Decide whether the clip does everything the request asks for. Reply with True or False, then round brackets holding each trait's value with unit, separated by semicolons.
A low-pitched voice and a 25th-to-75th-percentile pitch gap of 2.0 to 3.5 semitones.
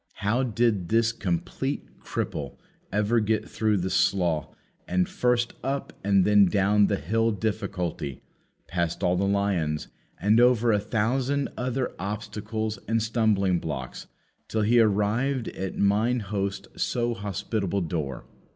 True (105 Hz; 3.2 semitones)